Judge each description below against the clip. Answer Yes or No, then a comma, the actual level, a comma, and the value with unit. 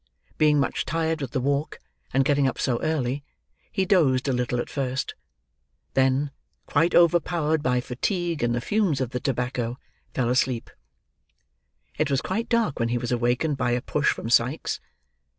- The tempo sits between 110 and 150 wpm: No, average, 170 wpm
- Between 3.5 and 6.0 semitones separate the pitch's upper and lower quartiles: Yes, average, 4.0 semitones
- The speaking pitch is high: No, low, 135 Hz